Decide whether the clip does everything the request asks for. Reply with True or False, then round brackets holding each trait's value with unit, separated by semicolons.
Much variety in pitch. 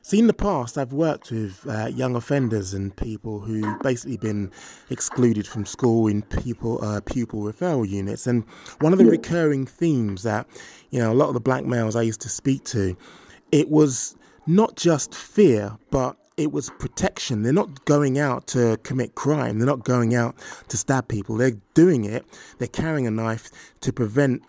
False (4.2 semitones)